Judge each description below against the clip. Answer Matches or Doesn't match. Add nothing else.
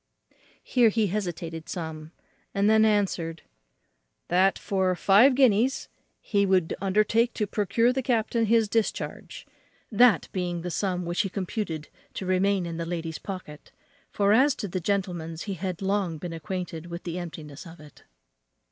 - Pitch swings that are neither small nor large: Matches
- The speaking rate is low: Doesn't match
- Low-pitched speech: Doesn't match